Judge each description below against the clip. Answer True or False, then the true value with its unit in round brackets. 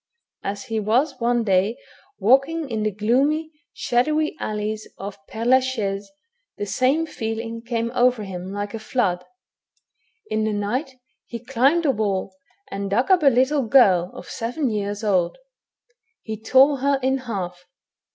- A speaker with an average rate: True (150 wpm)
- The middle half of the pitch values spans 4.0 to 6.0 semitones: True (4.3 semitones)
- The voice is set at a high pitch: True (230 Hz)